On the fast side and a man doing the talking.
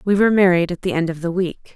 No: fast, 310 wpm; female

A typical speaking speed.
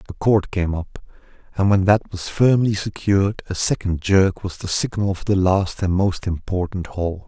Yes: average, 190 wpm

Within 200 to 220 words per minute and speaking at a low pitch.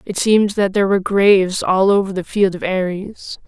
No: fast, 205 wpm; high, 195 Hz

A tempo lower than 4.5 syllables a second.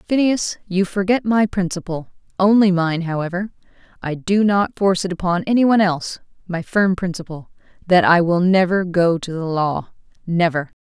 No: 5.0 syllables/s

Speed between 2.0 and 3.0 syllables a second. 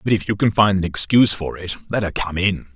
No: 5.9 syllables/s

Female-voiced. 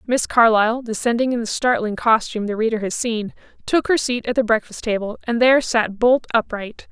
Yes: female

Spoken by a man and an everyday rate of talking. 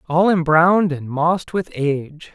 Yes: male; average, 155 wpm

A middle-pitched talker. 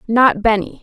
No: high, 220 Hz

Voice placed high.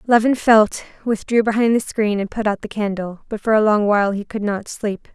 Yes: high, 215 Hz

